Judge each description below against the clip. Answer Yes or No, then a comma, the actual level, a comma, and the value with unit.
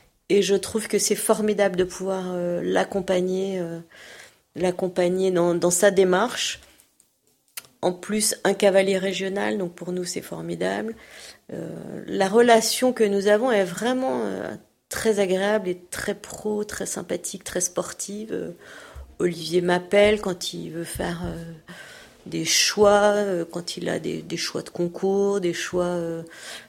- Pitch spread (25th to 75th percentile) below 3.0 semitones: Yes, narrow, 2.6 semitones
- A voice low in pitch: No, high, 190 Hz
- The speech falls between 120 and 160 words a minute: Yes, average, 150 wpm